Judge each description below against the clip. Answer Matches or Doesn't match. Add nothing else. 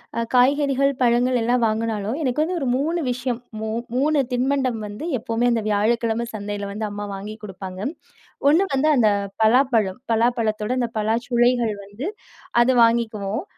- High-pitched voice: Matches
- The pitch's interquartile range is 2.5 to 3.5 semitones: Matches